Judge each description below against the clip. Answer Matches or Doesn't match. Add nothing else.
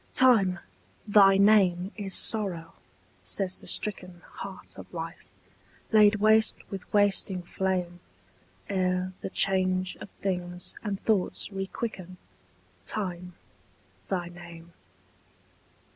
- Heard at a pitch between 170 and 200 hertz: Matches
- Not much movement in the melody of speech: Matches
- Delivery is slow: Matches